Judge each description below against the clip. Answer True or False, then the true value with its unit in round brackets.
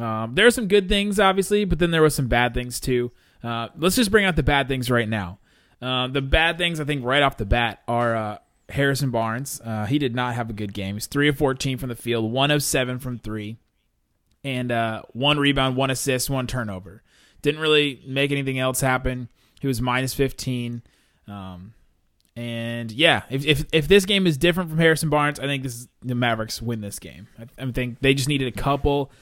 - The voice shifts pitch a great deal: False (3.7 semitones)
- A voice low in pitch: True (130 Hz)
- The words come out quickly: True (220 wpm)